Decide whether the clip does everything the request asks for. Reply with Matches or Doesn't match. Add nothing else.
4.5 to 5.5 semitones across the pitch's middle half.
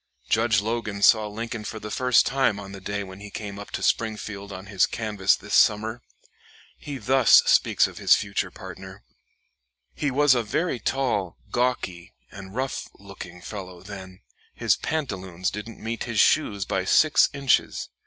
Doesn't match